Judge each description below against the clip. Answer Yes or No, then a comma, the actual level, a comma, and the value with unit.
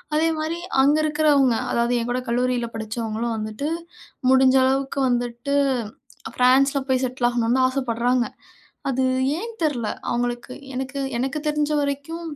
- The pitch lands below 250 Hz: No, very high, 260 Hz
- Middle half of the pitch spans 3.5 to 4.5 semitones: No, average, 2.8 semitones